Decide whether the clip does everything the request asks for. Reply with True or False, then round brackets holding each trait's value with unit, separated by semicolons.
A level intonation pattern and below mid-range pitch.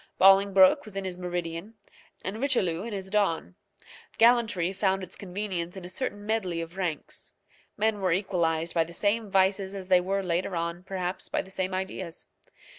False (2.3 semitones; 190 Hz)